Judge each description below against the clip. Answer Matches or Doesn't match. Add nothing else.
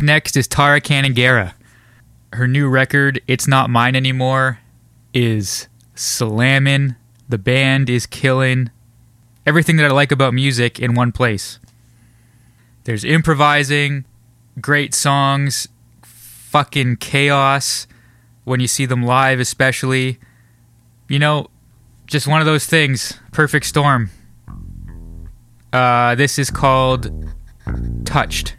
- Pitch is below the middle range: Matches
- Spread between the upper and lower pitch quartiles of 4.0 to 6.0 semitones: Doesn't match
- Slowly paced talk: Matches